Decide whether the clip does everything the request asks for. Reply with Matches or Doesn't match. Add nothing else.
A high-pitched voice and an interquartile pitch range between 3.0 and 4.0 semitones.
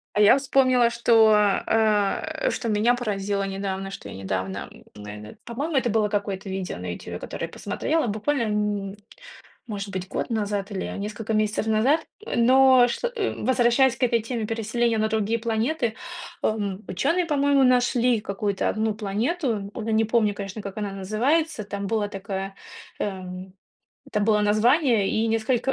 Matches